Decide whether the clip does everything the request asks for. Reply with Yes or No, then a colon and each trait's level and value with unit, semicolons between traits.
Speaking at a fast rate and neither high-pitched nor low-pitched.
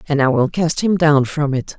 Yes: fast, 270 wpm; medium, 150 Hz